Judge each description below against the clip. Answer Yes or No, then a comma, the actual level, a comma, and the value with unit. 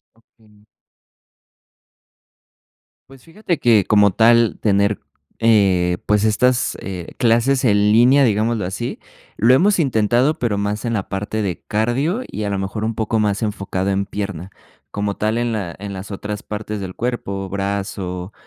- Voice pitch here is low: Yes, low, 105 Hz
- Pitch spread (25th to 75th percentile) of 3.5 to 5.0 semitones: No, average, 2.9 semitones